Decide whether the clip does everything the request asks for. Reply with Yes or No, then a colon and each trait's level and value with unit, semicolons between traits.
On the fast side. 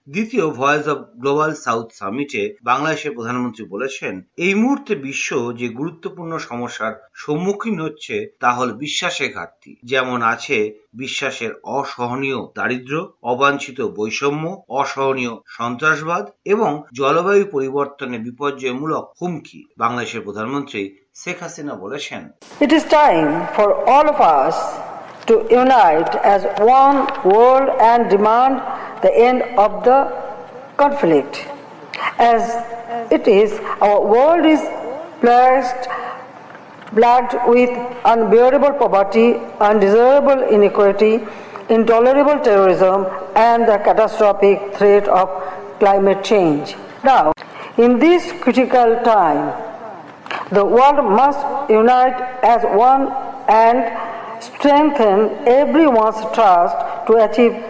No: average, 85 wpm